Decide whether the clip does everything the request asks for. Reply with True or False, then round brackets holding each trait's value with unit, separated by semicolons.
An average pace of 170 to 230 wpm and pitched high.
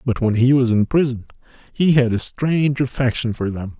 False (205 wpm; 125 Hz)